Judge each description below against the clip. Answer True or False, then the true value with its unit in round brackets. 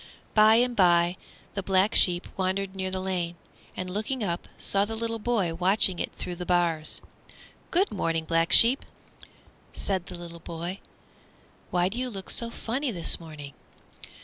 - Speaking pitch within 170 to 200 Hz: True (185 Hz)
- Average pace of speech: True (155 wpm)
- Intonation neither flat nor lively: True (3.9 semitones)